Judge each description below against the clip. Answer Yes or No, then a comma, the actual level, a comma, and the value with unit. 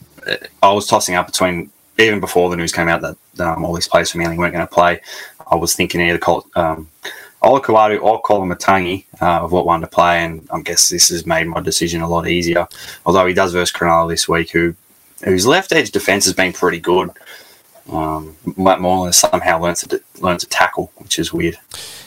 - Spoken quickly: Yes, fast, 220 wpm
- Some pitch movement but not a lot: No, narrow, 1.9 semitones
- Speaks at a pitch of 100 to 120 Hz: No, very low, 90 Hz